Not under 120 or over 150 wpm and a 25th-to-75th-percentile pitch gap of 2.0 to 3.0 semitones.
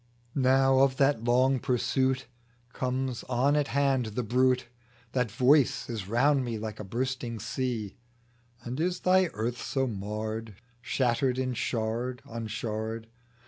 Yes: average, 140 wpm; average, 2.7 semitones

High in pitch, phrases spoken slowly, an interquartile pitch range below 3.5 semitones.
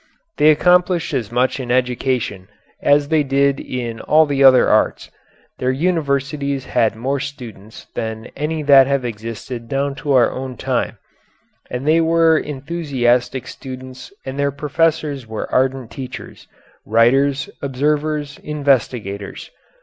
No: low, 135 Hz; slow, 130 wpm; average, 2.9 semitones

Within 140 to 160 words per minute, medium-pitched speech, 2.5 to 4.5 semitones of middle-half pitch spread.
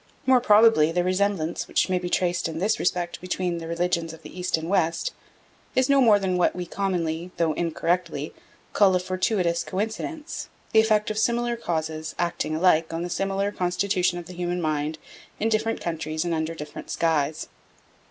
No: average, 180 wpm; medium, 180 Hz; average, 3.5 semitones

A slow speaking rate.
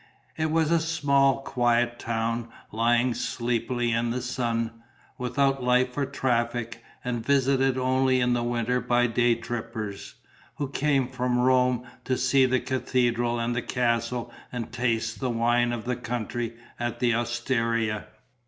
No: average, 145 wpm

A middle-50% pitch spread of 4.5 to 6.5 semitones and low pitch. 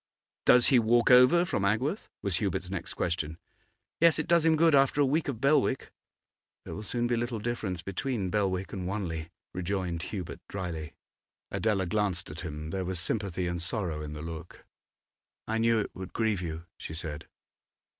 Yes: wide, 5.6 semitones; low, 100 Hz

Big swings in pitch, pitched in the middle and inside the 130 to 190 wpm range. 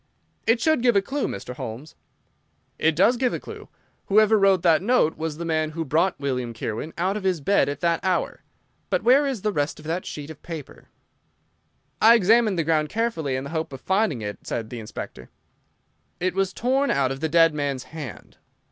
No: wide, 6.3 semitones; medium, 165 Hz; average, 200 wpm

